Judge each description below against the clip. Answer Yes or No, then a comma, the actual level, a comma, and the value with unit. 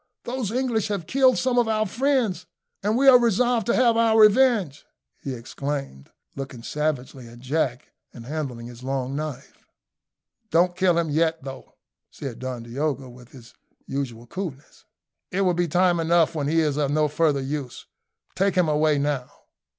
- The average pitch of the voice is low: No, medium, 155 Hz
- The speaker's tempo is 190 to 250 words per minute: No, average, 165 wpm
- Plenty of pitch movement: Yes, wide, 6.8 semitones